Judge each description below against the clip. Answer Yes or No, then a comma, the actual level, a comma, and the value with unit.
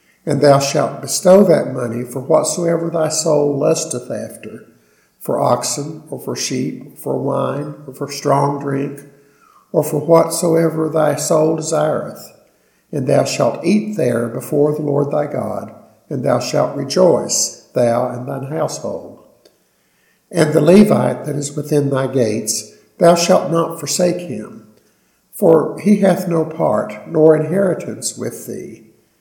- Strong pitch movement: No, average, 2.8 semitones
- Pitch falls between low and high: Yes, medium, 150 Hz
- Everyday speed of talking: Yes, average, 145 wpm